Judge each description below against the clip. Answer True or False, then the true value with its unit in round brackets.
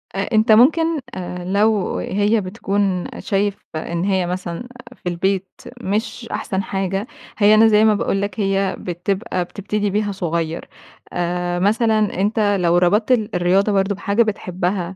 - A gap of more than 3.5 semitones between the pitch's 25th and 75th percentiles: False (2.8 semitones)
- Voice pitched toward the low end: False (195 Hz)